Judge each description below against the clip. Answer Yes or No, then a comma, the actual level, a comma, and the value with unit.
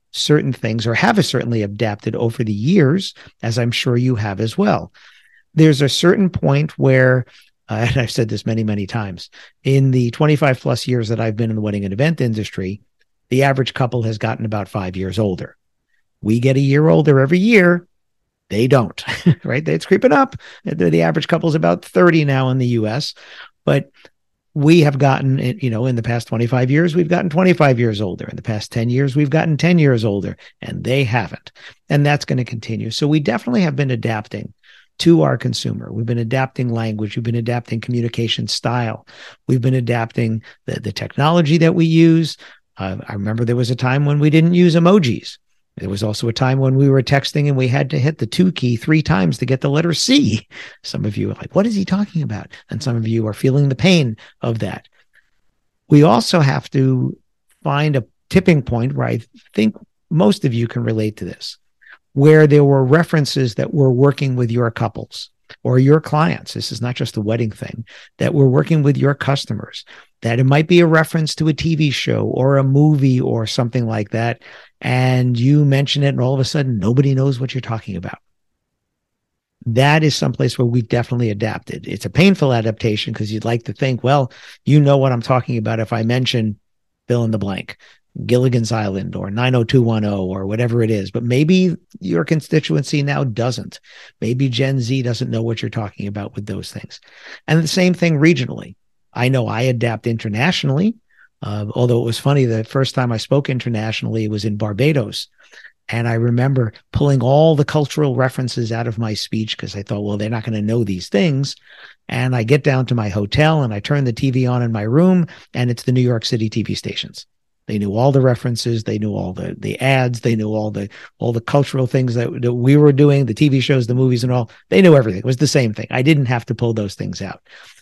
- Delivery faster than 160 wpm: Yes, fast, 205 wpm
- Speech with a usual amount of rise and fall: Yes, average, 4.2 semitones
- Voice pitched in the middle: No, low, 125 Hz